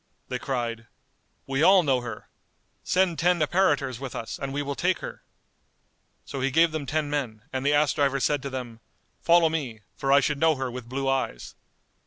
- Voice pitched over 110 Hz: Yes, medium, 140 Hz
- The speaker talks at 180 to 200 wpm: Yes, average, 195 wpm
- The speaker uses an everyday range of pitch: Yes, average, 3.3 semitones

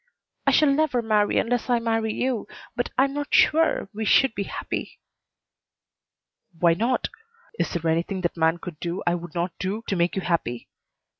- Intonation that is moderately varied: No, wide, 6.0 semitones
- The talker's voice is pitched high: Yes, high, 205 Hz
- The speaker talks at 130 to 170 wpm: No, average, 180 wpm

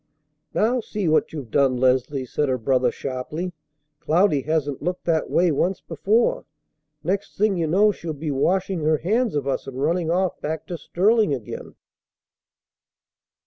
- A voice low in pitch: No, medium, 160 Hz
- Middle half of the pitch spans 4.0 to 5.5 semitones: Yes, average, 5.2 semitones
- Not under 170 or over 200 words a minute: No, average, 155 wpm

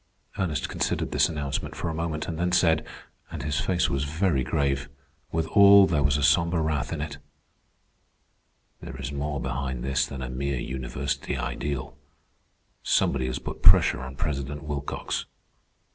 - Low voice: Yes, very low, 70 Hz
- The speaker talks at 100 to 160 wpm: Yes, average, 155 wpm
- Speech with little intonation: No, average, 3.0 semitones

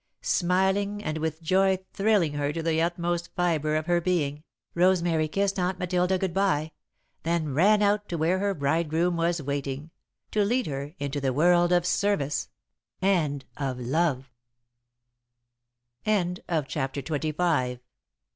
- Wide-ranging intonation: No, average, 3.8 semitones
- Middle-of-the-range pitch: Yes, medium, 170 Hz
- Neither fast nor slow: No, slow, 130 wpm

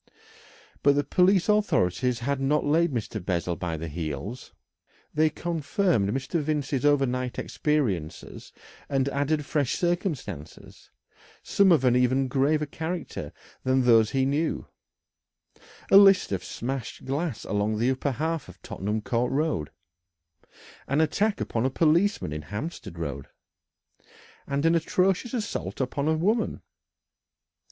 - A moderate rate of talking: No, slow, 130 wpm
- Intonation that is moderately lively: No, wide, 6.2 semitones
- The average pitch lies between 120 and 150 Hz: Yes, low, 135 Hz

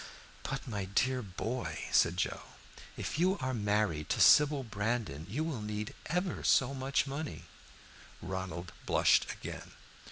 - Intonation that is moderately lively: No, wide, 6.2 semitones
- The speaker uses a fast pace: No, slow, 135 wpm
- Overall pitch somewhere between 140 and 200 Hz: No, low, 115 Hz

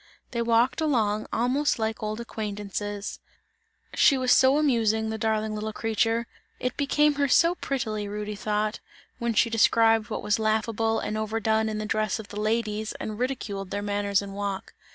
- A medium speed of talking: Yes, average, 170 wpm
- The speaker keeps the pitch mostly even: Yes, narrow, 1.9 semitones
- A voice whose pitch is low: No, high, 220 Hz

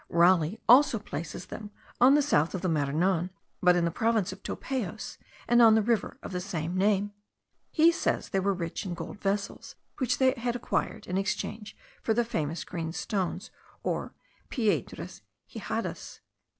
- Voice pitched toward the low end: No, high, 200 Hz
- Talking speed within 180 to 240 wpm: No, average, 165 wpm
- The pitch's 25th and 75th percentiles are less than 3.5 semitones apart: No, average, 4.8 semitones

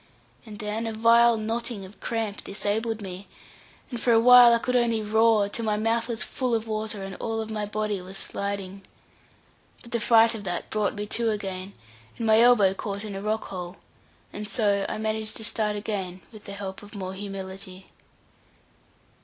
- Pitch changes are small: Yes, narrow, 2.2 semitones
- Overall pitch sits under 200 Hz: No, high, 215 Hz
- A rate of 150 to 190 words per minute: Yes, average, 185 wpm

